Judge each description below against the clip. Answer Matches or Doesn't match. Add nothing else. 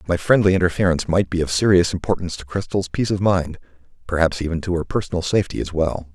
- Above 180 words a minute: Matches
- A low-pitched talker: Matches